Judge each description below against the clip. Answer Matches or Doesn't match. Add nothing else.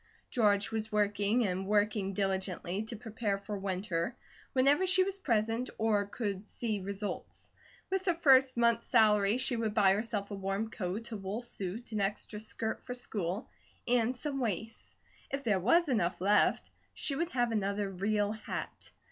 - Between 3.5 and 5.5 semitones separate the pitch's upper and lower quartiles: Doesn't match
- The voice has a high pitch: Matches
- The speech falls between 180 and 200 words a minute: Doesn't match